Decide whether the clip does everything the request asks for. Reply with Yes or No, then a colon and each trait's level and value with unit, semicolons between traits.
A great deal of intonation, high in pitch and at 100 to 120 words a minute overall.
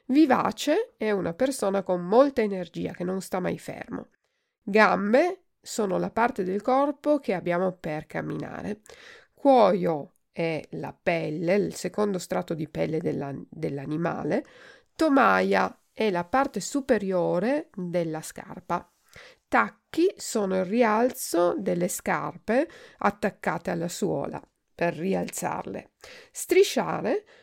Yes: wide, 7.5 semitones; high, 205 Hz; slow, 115 wpm